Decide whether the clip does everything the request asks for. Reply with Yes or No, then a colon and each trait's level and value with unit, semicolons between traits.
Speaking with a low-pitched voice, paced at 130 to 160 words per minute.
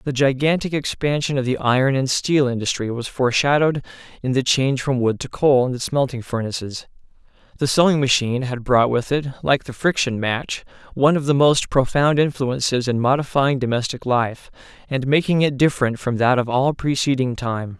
No: low, 130 Hz; average, 180 wpm